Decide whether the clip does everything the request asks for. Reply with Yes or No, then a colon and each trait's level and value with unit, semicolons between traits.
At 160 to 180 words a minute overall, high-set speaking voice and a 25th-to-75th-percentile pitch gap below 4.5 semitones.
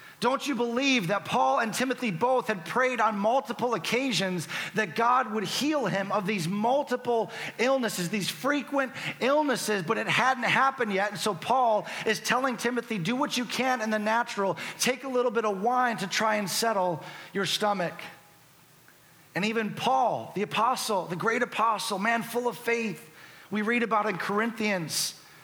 Yes: average, 170 wpm; high, 220 Hz; average, 3.8 semitones